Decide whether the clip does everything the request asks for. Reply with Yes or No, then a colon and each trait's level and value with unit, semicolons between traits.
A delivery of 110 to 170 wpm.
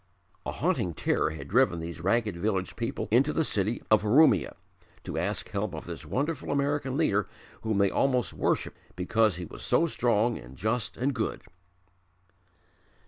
Yes: average, 160 wpm